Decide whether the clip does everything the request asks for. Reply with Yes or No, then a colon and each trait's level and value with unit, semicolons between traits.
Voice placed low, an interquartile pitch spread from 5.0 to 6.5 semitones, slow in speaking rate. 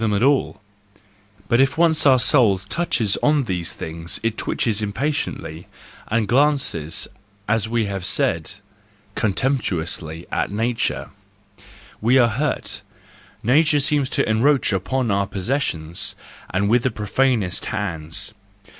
Yes: low, 110 Hz; wide, 5.5 semitones; slow, 130 wpm